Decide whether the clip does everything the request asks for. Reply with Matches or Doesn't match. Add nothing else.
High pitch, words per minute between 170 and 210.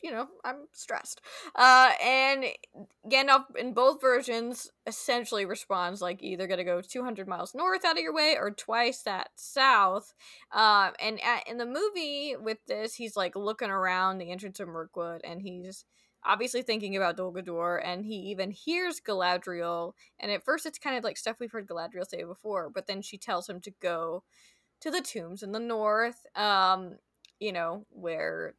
Matches